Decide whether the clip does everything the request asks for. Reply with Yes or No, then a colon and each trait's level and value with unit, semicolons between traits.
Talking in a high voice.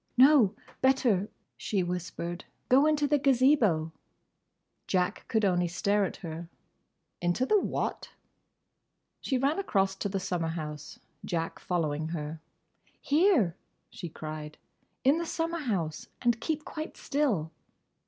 Yes: high, 195 Hz